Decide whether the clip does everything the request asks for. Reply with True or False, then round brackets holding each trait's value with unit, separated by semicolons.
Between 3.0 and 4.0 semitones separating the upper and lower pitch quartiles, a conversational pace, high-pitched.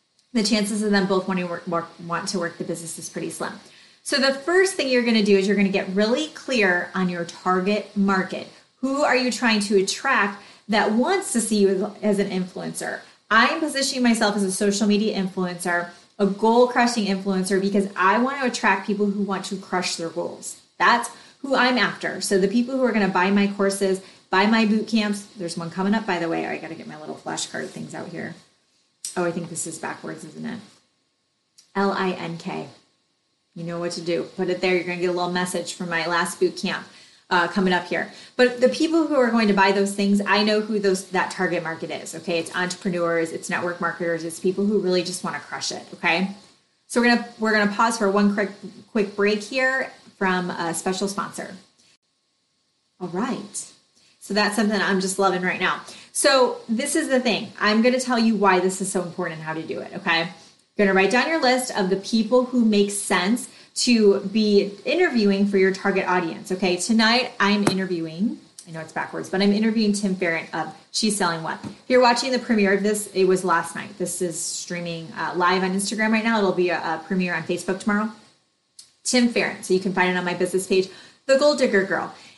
False (3.4 semitones; 220 wpm; 195 Hz)